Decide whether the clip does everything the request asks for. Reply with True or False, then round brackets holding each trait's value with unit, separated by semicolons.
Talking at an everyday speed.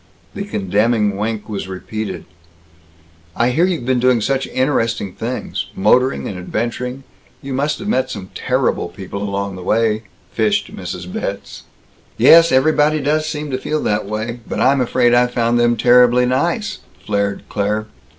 True (155 wpm)